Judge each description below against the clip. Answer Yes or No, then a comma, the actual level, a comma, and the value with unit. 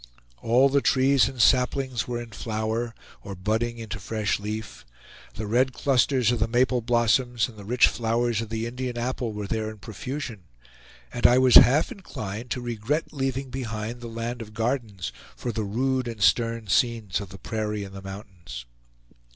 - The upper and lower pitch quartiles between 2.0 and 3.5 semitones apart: Yes, average, 2.7 semitones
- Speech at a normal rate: Yes, average, 175 wpm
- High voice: No, low, 115 Hz